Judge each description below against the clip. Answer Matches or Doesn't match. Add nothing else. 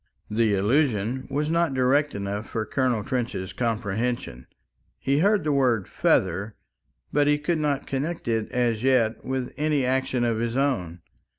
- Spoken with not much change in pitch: Doesn't match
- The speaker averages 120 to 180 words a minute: Matches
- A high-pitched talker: Doesn't match